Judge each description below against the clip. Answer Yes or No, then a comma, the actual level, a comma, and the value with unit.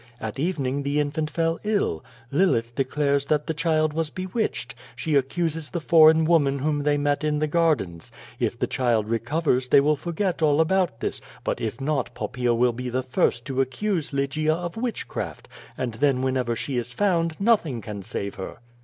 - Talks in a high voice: No, medium, 145 Hz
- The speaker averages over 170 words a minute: Yes, average, 185 wpm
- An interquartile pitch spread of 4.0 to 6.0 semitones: Yes, average, 4.3 semitones